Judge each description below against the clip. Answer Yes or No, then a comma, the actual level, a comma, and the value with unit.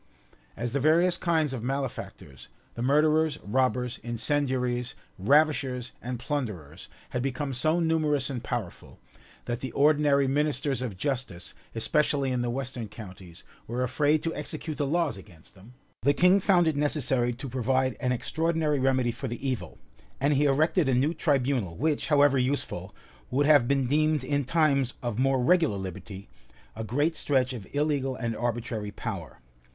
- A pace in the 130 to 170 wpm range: Yes, average, 155 wpm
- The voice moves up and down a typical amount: Yes, average, 3.6 semitones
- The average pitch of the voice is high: No, low, 135 Hz